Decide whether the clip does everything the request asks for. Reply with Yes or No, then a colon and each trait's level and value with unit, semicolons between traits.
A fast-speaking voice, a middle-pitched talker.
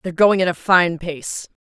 Yes: fast, 220 wpm; medium, 175 Hz